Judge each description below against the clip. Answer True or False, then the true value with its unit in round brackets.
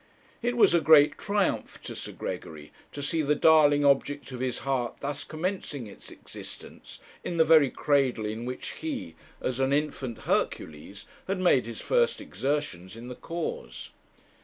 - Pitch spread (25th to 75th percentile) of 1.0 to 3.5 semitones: False (4.5 semitones)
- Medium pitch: True (145 Hz)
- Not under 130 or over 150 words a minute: False (160 wpm)